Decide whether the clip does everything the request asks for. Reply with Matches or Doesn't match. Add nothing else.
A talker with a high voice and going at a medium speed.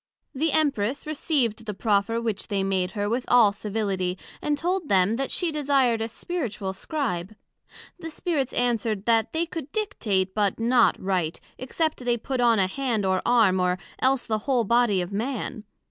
Matches